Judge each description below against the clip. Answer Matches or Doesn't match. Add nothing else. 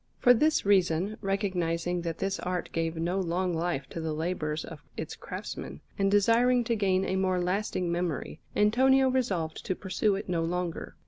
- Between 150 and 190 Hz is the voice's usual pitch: Matches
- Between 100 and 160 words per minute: Doesn't match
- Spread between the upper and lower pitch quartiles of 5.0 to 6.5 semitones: Doesn't match